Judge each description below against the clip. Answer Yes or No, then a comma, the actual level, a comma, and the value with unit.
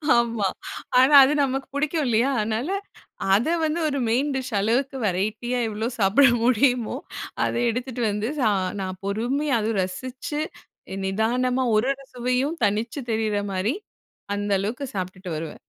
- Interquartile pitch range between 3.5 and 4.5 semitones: Yes, average, 4.0 semitones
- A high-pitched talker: Yes, high, 235 Hz